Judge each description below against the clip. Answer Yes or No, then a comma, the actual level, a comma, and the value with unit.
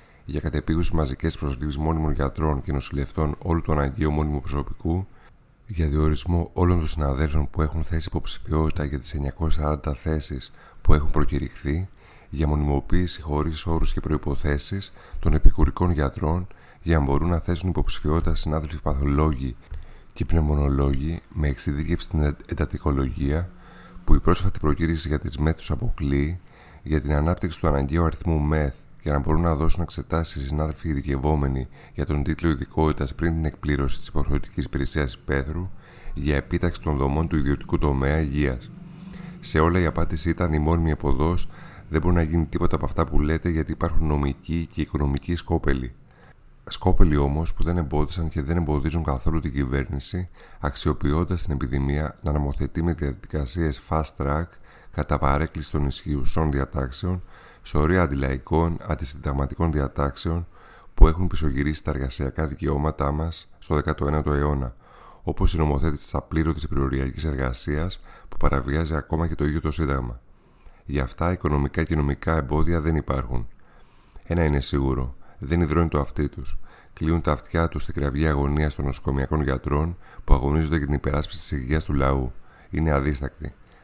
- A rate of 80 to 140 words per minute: No, average, 150 wpm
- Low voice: Yes, very low, 75 Hz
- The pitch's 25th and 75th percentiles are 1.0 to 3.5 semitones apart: Yes, average, 2.7 semitones